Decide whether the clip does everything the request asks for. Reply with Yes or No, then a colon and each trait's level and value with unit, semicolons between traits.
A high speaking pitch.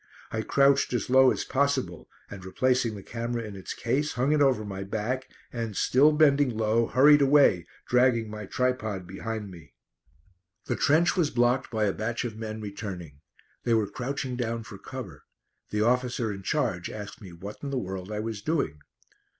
No: low, 115 Hz